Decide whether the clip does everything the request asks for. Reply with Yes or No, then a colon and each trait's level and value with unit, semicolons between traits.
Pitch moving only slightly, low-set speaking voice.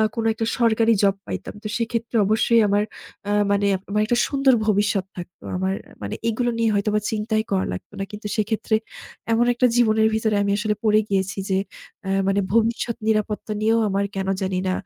No: narrow, 2.1 semitones; high, 215 Hz